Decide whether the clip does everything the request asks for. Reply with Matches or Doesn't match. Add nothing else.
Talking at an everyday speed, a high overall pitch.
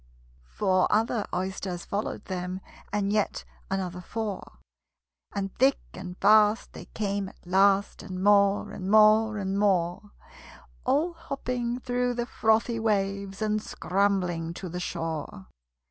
Doesn't match